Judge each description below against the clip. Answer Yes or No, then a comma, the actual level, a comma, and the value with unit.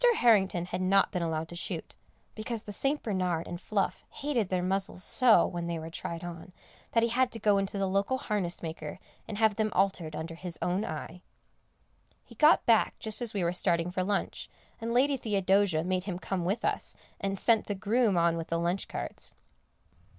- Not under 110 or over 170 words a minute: No, average, 200 wpm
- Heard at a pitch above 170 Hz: Yes, high, 190 Hz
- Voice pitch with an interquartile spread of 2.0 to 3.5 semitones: No, average, 3.9 semitones